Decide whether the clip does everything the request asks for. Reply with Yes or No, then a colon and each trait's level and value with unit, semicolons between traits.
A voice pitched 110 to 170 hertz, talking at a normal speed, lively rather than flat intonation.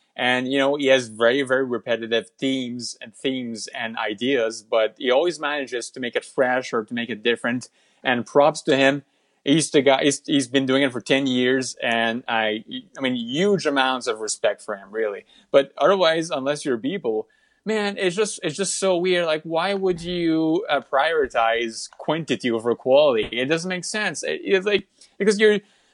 Yes: medium, 140 Hz; average, 190 wpm; wide, 7.1 semitones